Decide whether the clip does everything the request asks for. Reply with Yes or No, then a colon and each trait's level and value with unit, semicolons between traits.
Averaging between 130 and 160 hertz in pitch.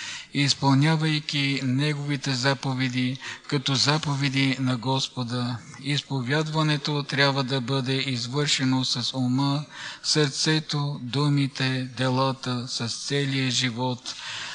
Yes: low, 135 Hz